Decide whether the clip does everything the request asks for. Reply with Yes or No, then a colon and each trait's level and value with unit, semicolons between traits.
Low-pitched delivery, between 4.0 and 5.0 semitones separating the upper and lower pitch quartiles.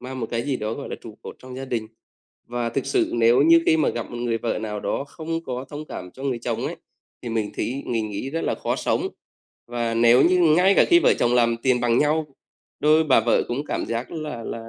Yes: low, 125 Hz; average, 4.3 semitones